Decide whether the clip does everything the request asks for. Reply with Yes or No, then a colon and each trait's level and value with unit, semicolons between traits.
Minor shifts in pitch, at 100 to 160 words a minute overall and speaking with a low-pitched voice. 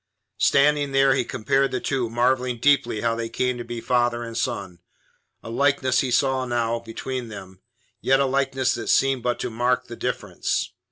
No: narrow, 2.3 semitones; average, 180 wpm; low, 125 Hz